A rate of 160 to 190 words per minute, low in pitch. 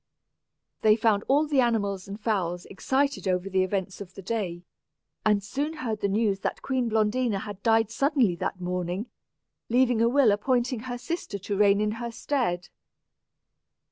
No: average, 165 wpm; high, 215 Hz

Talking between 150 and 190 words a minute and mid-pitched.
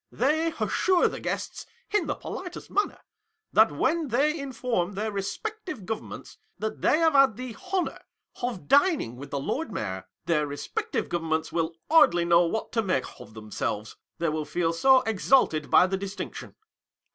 No: average, 165 wpm; high, 215 Hz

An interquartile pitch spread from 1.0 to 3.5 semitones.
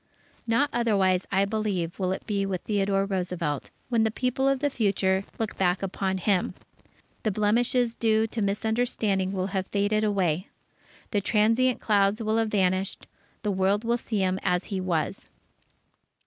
Yes: average, 2.7 semitones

